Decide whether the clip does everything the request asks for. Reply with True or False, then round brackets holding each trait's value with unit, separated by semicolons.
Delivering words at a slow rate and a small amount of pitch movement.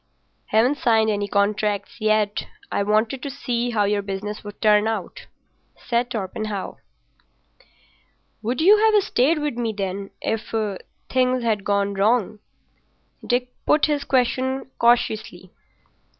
False (115 wpm; 3.4 semitones)